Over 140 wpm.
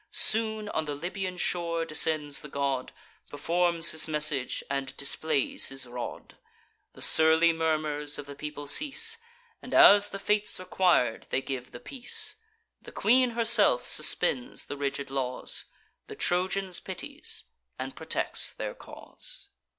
No: slow, 135 wpm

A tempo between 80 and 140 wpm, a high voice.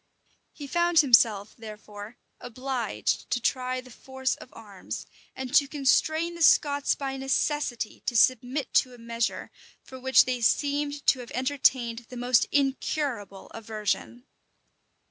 Yes: slow, 135 wpm; very high, 255 Hz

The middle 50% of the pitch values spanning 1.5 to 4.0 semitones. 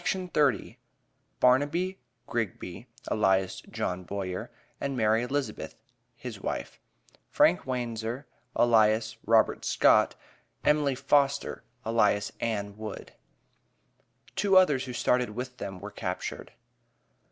No: average, 4.6 semitones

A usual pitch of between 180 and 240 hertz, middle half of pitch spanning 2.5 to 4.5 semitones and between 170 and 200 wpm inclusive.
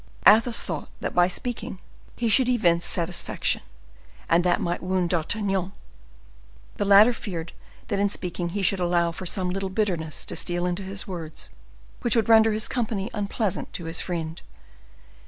No: high, 190 Hz; average, 3.3 semitones; average, 155 wpm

